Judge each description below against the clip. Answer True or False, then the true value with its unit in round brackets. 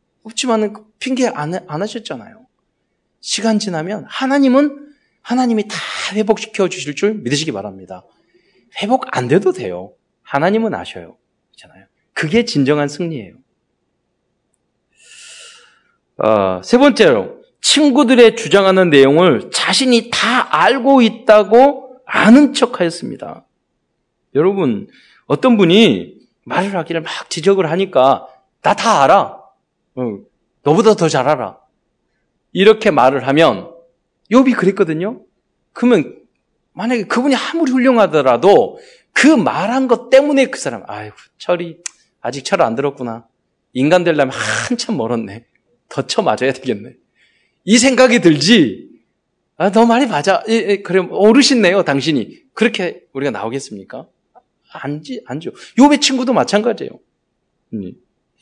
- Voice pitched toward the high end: True (215 Hz)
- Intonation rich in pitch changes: True (7.2 semitones)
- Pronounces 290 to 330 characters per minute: False (255 characters per minute)